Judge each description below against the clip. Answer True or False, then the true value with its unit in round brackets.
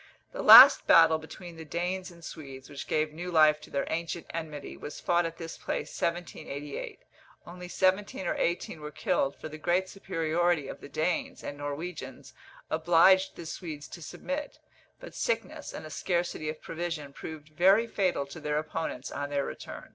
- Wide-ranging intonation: False (2.7 semitones)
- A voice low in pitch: False (165 Hz)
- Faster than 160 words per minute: True (175 wpm)